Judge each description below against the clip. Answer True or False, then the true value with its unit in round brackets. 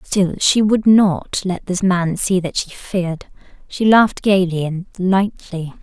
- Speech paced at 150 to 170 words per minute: True (165 wpm)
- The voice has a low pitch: False (190 Hz)